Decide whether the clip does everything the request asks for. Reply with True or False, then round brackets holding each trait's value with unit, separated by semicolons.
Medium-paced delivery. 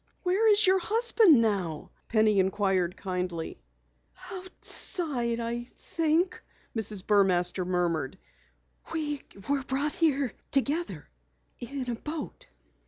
False (105 wpm)